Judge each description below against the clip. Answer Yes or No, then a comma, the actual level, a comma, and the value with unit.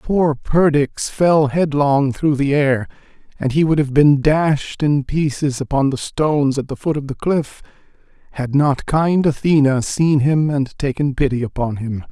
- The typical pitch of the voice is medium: Yes, medium, 145 Hz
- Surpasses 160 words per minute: Yes, average, 175 wpm